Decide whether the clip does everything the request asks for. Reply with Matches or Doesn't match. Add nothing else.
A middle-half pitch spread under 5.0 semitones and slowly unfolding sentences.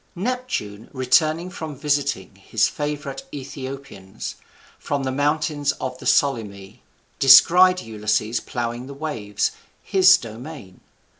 Doesn't match